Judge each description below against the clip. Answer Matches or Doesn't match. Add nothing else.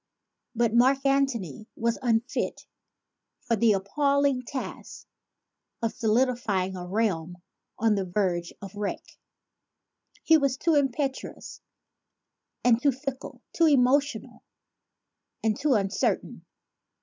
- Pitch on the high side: Matches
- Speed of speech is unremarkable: Doesn't match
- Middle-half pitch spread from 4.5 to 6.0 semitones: Matches